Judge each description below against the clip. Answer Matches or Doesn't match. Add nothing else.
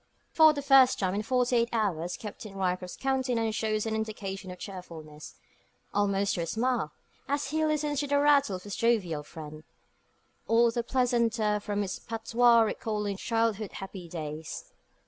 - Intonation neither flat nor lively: Matches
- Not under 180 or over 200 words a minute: Doesn't match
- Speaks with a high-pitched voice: Matches